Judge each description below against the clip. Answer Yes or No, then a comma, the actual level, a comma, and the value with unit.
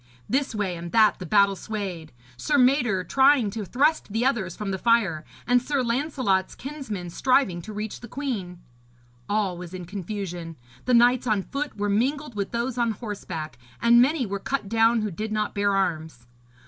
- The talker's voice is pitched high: Yes, high, 215 Hz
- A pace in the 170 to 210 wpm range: Yes, average, 180 wpm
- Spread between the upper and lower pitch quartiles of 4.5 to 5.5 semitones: Yes, average, 4.8 semitones